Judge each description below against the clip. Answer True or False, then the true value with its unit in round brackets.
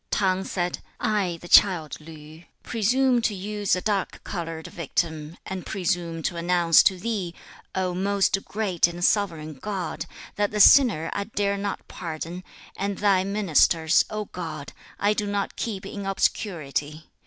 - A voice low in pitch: False (185 Hz)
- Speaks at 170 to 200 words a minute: False (155 wpm)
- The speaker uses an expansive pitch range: False (3.4 semitones)